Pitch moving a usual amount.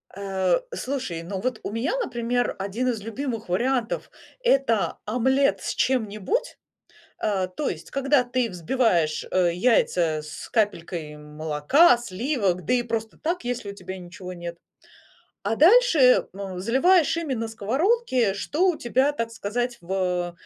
No: wide, 6.1 semitones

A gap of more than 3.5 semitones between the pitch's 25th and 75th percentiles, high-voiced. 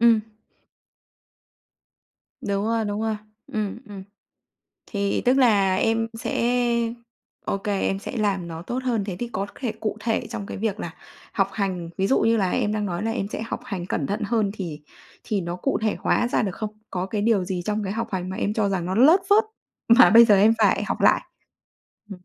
No: average, 2.8 semitones; high, 210 Hz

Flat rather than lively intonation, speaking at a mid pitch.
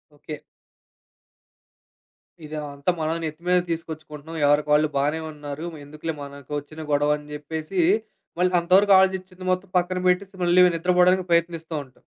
No: average, 3.4 semitones; medium, 160 Hz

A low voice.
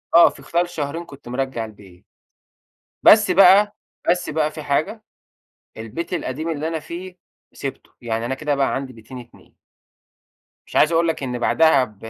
No: medium, 150 Hz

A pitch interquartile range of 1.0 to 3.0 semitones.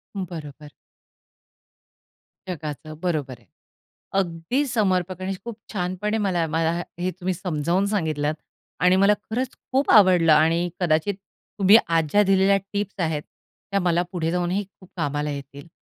No: average, 3.8 semitones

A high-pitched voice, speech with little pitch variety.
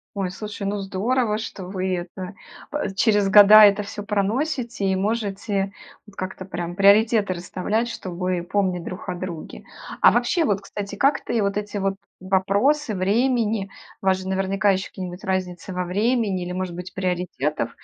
Yes: high, 195 Hz; narrow, 2.2 semitones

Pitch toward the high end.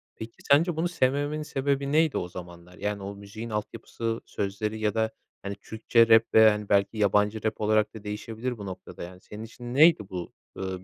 No: low, 110 Hz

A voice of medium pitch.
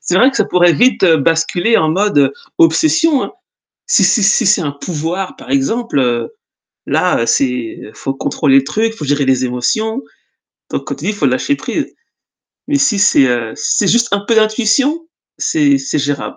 Yes: medium, 180 Hz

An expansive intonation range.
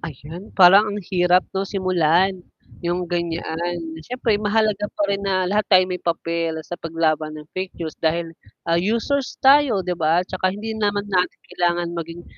No: average, 3.3 semitones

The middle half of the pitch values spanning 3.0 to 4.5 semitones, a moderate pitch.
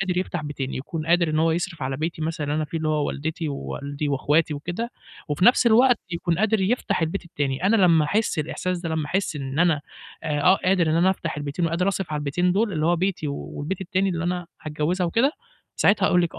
Yes: average, 3.5 semitones; medium, 165 Hz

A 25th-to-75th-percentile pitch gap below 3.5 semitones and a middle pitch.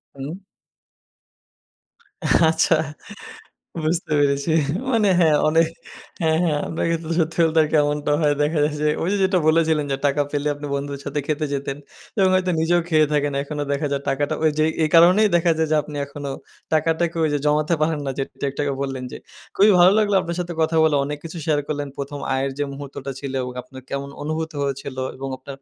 Yes: narrow, 2.6 semitones; medium, 150 Hz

